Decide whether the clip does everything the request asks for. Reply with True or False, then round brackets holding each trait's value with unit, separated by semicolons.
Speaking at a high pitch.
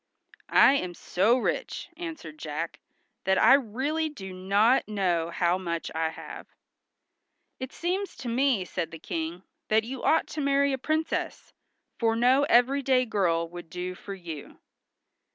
True (215 Hz)